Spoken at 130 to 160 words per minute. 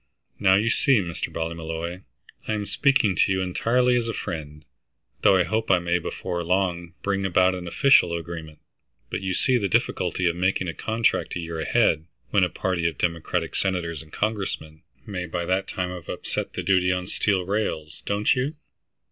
No: average, 185 wpm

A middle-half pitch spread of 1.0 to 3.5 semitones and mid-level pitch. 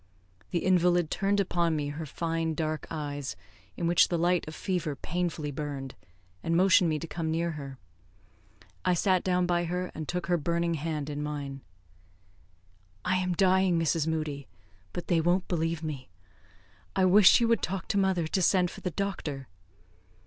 Yes: average, 2.8 semitones; medium, 170 Hz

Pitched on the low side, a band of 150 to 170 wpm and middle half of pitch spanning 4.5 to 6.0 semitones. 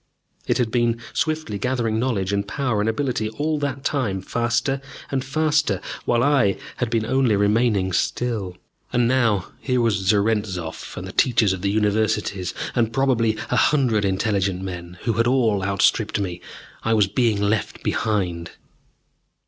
No: low, 110 Hz; average, 155 wpm; average, 3.8 semitones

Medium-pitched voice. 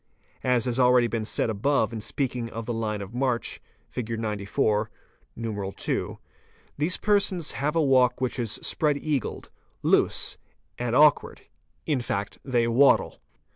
No: low, 120 Hz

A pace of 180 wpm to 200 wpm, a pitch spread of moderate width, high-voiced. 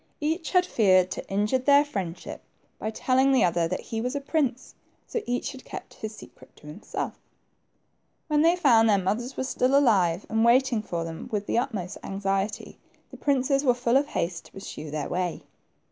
No: average, 190 wpm; wide, 5.8 semitones; high, 225 Hz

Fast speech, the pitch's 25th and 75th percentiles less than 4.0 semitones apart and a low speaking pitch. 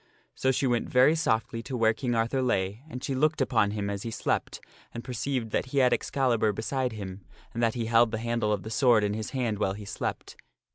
Yes: fast, 235 wpm; average, 3.0 semitones; low, 115 Hz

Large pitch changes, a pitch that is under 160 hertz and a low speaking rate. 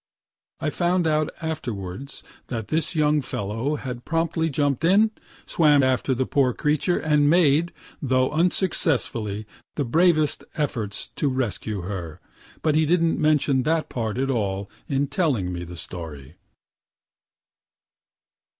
Yes: wide, 5.8 semitones; medium, 140 Hz; slow, 130 wpm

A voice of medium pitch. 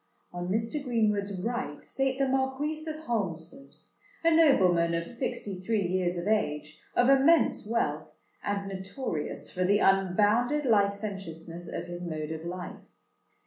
No: high, 200 Hz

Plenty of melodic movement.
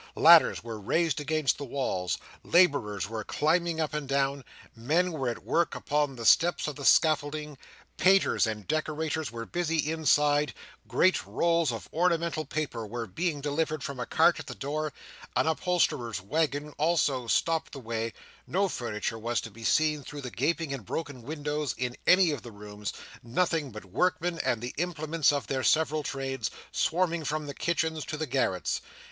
No: average, 4.6 semitones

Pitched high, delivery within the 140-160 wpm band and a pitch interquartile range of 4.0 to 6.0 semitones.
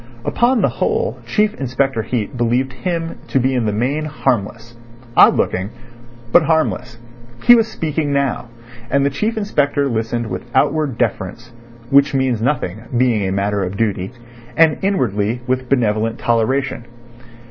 No: low, 125 Hz; average, 145 wpm; average, 4.4 semitones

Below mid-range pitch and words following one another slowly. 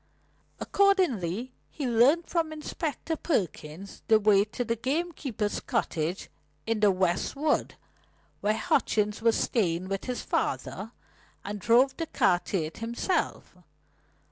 No: high, 225 Hz; slow, 125 wpm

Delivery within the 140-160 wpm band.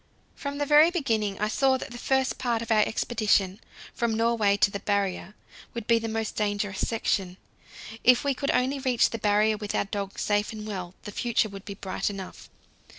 No: average, 200 wpm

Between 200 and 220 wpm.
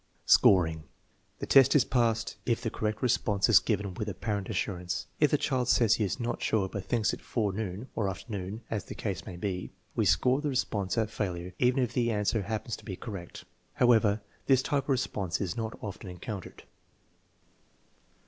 No: average, 185 wpm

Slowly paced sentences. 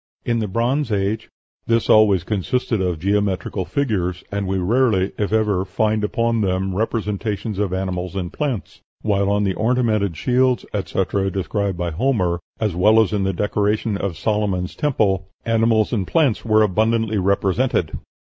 No: average, 155 wpm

